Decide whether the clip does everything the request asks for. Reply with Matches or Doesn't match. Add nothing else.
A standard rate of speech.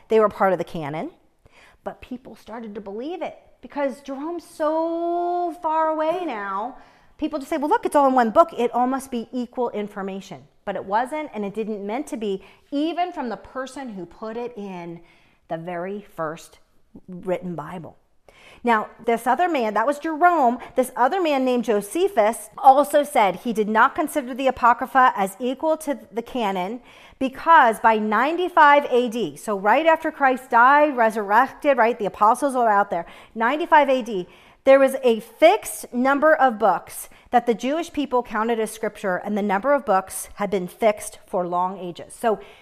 Matches